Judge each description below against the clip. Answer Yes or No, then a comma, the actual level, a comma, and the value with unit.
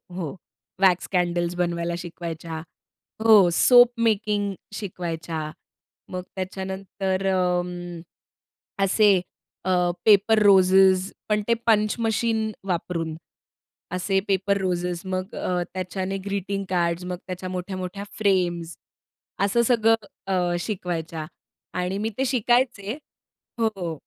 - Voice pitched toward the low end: No, medium, 185 Hz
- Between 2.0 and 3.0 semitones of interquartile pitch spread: Yes, narrow, 2.5 semitones